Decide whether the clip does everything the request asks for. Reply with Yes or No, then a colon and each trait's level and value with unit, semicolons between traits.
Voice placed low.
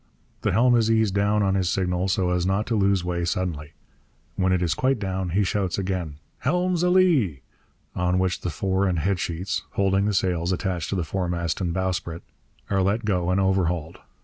Yes: very low, 95 Hz